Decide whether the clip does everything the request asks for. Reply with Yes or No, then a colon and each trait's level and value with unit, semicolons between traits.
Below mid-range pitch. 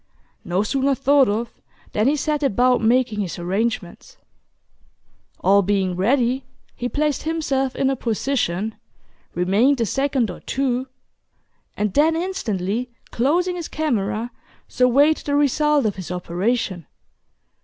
No: high, 245 Hz